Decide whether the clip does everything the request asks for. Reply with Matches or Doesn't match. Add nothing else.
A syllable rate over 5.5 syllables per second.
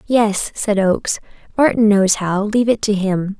Doesn't match